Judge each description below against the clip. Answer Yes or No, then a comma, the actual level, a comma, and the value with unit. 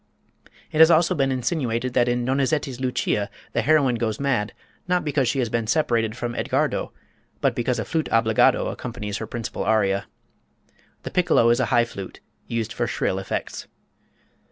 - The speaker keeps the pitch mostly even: No, average, 3.5 semitones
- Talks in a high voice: No, low, 120 Hz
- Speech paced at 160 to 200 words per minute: Yes, average, 165 wpm